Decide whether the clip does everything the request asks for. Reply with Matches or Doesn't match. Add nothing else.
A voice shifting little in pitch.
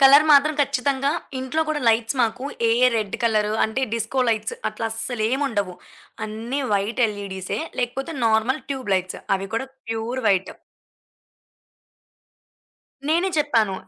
Doesn't match